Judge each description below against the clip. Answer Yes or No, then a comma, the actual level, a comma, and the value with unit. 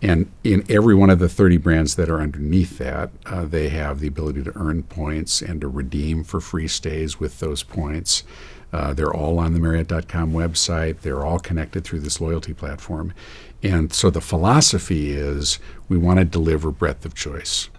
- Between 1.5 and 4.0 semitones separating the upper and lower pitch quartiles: Yes, average, 2.8 semitones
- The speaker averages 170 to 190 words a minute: Yes, average, 185 wpm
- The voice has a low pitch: Yes, very low, 80 Hz